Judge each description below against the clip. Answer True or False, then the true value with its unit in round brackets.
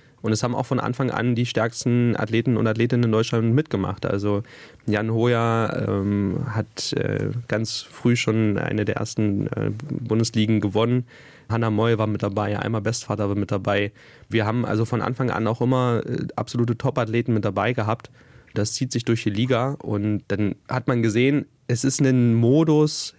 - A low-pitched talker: True (115 Hz)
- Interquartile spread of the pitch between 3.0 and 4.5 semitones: False (2.5 semitones)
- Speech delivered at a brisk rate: False (175 wpm)